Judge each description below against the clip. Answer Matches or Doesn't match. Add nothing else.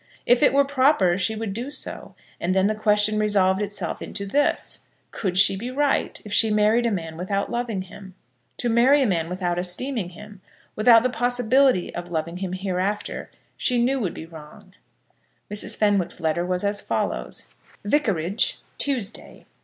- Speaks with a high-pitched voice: Matches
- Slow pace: Doesn't match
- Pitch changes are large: Doesn't match